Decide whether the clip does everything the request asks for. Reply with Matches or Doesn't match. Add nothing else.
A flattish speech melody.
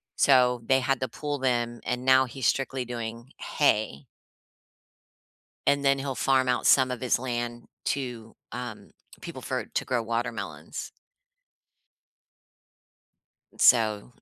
Matches